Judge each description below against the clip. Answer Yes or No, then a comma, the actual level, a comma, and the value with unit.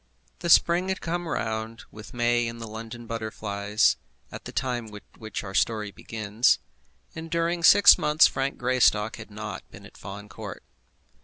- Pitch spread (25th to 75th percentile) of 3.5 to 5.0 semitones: Yes, average, 4.1 semitones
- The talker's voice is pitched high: No, low, 115 Hz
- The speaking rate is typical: Yes, average, 165 wpm